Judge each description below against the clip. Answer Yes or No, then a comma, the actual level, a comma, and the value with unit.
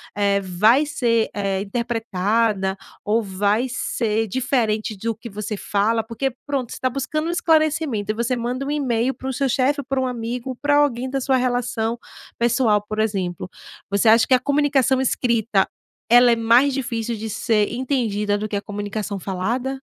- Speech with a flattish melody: No, average, 3.6 semitones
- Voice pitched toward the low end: No, high, 235 Hz